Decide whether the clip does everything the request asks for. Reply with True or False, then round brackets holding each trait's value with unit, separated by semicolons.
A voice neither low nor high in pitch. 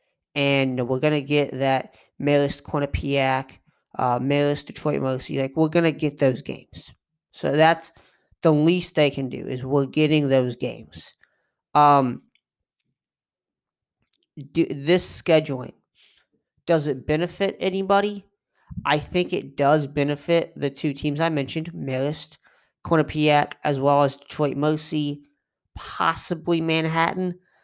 True (150 Hz)